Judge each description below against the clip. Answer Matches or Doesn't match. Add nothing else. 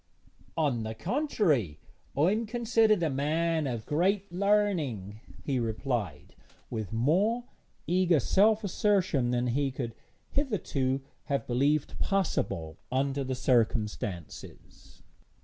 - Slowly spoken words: Matches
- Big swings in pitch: Matches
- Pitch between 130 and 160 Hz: Matches